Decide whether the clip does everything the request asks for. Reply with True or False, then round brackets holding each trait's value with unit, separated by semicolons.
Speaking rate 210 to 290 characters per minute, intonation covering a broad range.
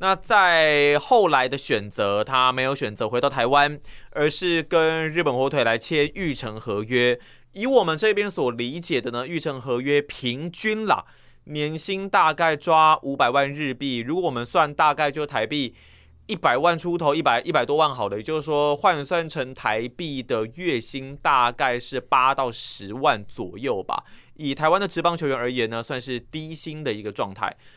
False (260 characters per minute; 4.5 semitones)